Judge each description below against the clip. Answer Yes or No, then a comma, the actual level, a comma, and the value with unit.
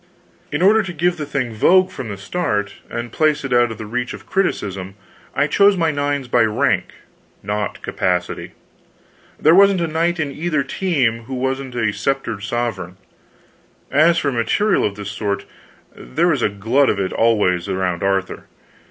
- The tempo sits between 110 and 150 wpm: No, average, 170 wpm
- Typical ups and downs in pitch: No, wide, 7.4 semitones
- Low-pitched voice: Yes, low, 125 Hz